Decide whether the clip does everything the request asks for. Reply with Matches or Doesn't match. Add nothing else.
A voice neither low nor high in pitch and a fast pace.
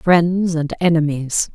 Doesn't match